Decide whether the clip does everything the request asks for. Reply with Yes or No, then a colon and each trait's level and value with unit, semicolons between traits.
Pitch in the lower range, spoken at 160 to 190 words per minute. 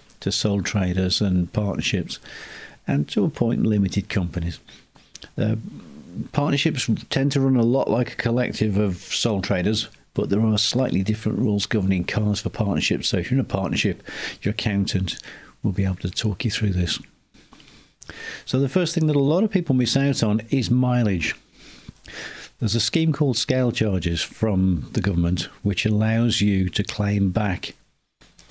Yes: low, 105 Hz; average, 165 wpm